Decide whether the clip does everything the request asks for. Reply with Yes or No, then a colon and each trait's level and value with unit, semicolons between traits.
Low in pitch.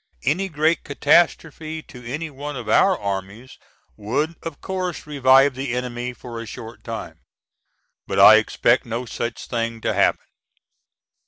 Yes: low, 130 Hz